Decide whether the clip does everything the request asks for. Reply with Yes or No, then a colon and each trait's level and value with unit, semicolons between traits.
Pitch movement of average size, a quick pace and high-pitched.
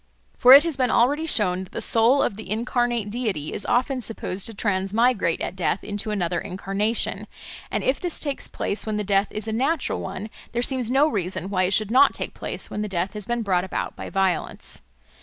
Yes: average, 4.2 semitones; fast, 215 wpm; high, 215 Hz